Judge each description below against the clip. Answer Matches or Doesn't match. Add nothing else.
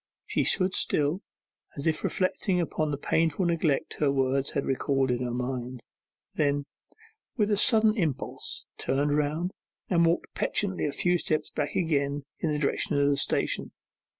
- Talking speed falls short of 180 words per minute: Matches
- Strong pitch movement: Doesn't match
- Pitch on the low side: Doesn't match